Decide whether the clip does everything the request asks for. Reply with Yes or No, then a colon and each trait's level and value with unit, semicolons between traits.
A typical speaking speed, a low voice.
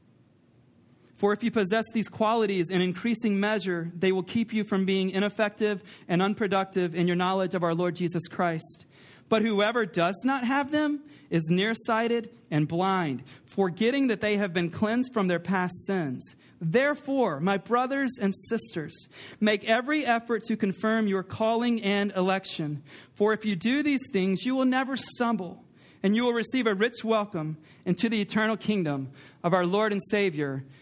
No: average, 165 wpm; high, 205 Hz